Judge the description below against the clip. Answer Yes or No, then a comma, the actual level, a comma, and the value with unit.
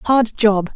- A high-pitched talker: Yes, high, 220 Hz